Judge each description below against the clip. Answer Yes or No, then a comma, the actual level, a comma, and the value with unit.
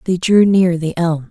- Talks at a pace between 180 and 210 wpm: No, fast, 230 wpm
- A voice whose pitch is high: No, medium, 175 Hz